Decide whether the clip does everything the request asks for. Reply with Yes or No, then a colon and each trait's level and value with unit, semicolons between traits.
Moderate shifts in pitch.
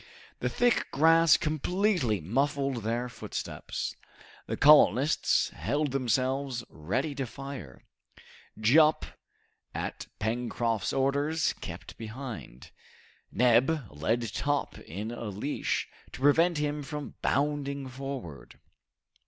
Yes: average, 4.1 semitones